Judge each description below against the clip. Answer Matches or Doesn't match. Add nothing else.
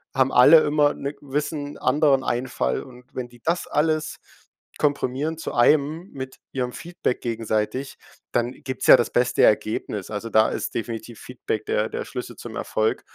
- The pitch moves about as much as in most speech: Matches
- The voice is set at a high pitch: Doesn't match